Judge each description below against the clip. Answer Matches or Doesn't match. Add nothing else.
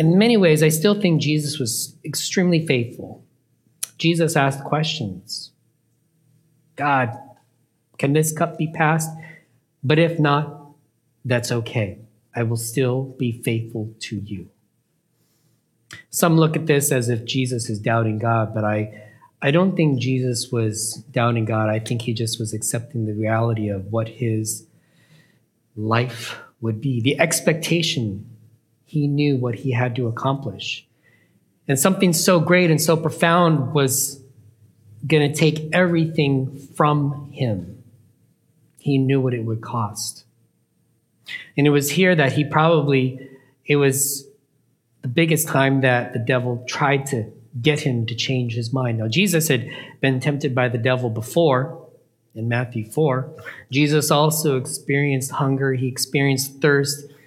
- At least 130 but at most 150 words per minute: Matches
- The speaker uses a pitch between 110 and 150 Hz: Matches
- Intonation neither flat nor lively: Matches